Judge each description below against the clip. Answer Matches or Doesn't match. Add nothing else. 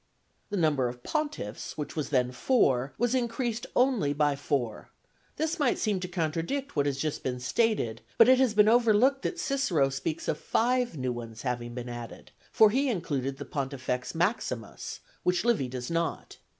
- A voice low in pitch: Doesn't match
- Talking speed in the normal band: Matches